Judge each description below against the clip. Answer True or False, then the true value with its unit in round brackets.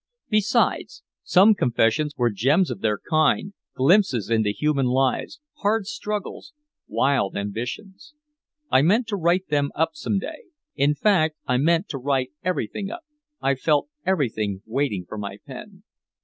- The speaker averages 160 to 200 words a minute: False (145 wpm)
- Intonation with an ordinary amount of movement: False (7.7 semitones)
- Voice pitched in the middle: True (150 Hz)